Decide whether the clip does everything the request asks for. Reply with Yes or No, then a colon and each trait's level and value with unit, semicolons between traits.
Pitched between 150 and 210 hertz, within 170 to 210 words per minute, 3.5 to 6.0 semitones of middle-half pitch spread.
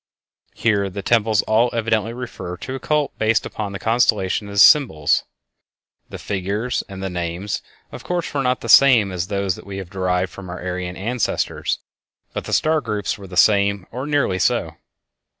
No: low, 100 Hz; average, 180 wpm; average, 4.0 semitones